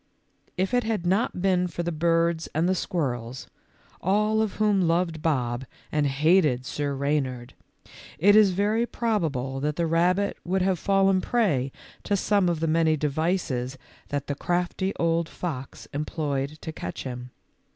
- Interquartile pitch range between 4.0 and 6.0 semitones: Yes, average, 5.0 semitones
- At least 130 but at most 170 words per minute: Yes, average, 160 wpm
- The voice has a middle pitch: Yes, medium, 165 Hz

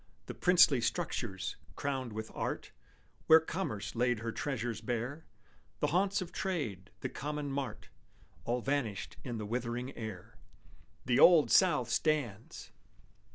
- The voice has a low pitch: Yes, low, 125 Hz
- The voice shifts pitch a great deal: No, average, 4.9 semitones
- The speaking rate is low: Yes, slow, 130 wpm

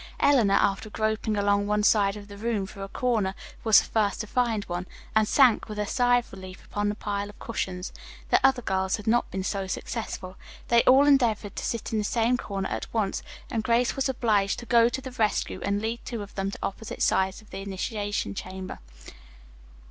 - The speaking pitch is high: Yes, high, 210 Hz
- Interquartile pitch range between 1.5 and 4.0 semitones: Yes, average, 2.9 semitones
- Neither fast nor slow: No, fast, 210 wpm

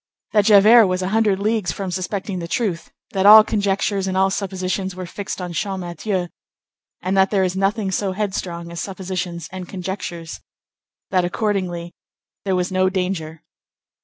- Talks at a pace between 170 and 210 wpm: No, average, 160 wpm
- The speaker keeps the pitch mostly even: Yes, narrow, 1.8 semitones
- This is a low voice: No, high, 190 Hz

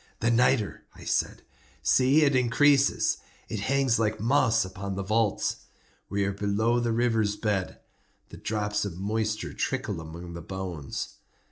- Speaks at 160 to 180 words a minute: No, average, 145 wpm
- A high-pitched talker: No, low, 110 Hz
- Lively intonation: No, average, 3.3 semitones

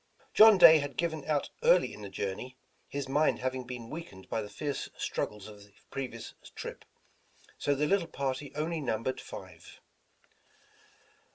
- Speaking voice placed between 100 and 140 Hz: Yes, low, 135 Hz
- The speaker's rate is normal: Yes, average, 155 wpm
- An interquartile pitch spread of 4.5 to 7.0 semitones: Yes, average, 5.2 semitones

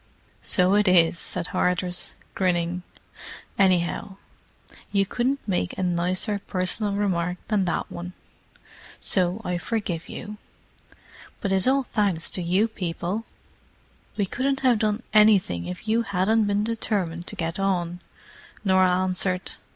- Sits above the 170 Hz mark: Yes, medium, 185 Hz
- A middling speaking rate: No, slow, 130 wpm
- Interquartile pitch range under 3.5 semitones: Yes, average, 2.9 semitones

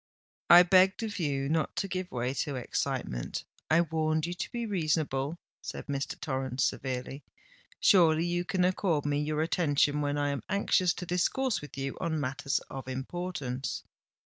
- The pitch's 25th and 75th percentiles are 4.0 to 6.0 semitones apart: Yes, average, 4.5 semitones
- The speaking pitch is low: No, medium, 155 Hz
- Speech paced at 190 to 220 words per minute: No, average, 160 wpm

